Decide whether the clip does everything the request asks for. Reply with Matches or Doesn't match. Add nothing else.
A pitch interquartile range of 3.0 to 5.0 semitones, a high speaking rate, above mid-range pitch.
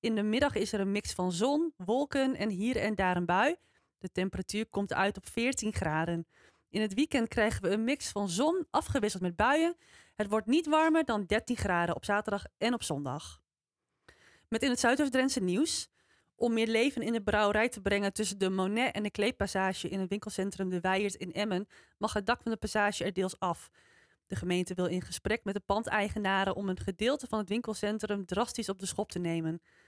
Matches